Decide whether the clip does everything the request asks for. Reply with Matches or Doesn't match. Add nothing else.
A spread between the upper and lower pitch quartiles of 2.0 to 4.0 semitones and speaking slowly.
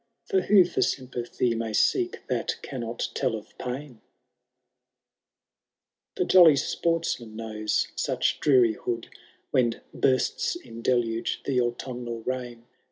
Matches